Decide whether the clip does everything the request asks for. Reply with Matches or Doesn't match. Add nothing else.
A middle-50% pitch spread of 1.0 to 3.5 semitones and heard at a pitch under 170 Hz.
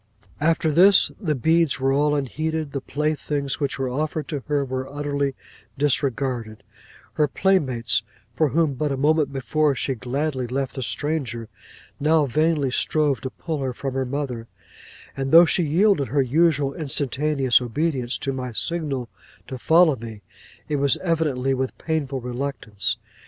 Matches